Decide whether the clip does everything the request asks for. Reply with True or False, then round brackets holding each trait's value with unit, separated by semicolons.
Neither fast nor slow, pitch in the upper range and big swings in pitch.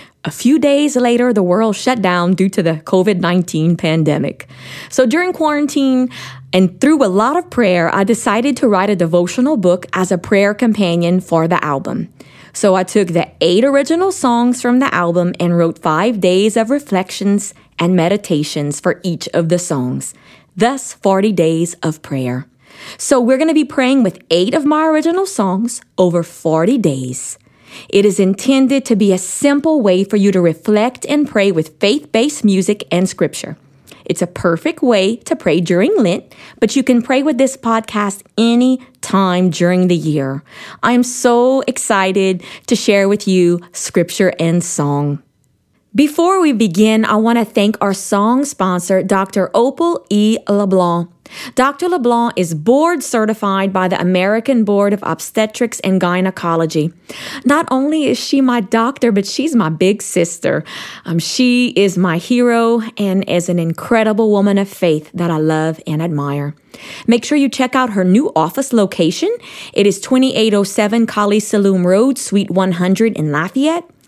True (165 wpm; 200 Hz; 5.9 semitones)